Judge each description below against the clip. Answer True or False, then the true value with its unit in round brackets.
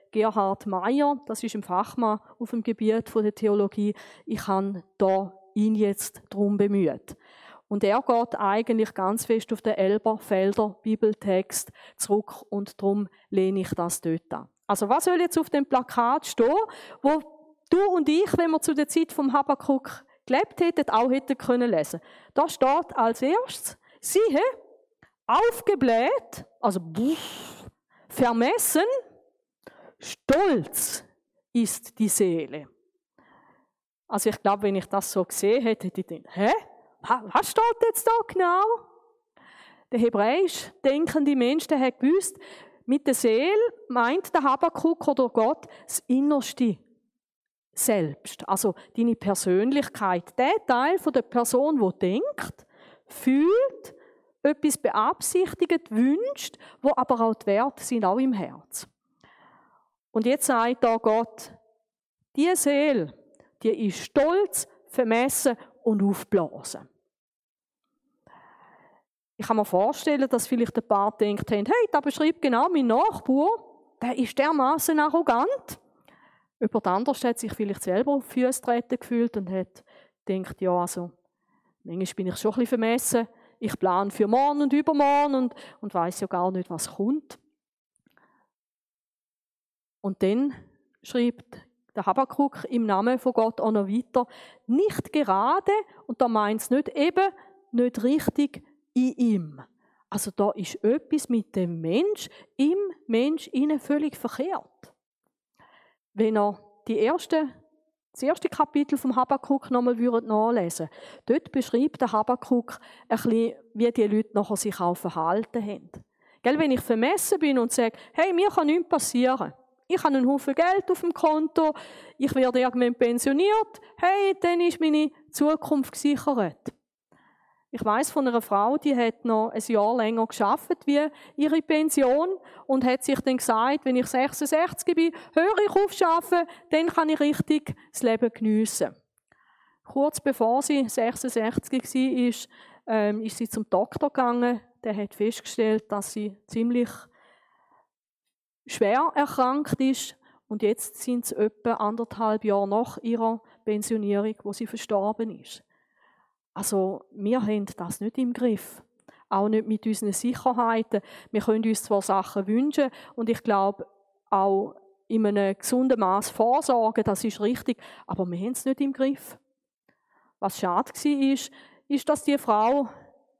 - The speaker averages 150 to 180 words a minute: False (140 wpm)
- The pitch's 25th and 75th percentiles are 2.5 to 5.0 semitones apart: False (5.5 semitones)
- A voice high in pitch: True (245 Hz)